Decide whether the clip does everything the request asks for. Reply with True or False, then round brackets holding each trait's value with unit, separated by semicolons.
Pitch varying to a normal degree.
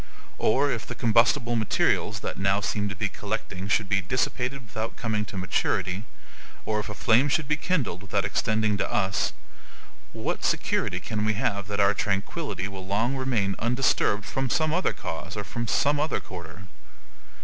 True (4.3 semitones)